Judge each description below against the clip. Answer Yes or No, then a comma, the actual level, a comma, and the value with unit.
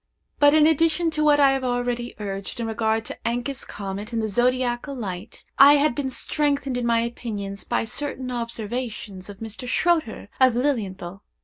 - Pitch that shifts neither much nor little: Yes, average, 4.1 semitones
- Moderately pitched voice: No, high, 240 Hz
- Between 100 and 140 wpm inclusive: No, average, 175 wpm